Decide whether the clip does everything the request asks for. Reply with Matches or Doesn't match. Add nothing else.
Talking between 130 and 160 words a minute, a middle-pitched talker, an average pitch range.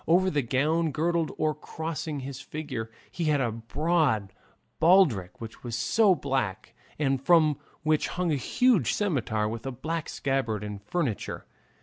Doesn't match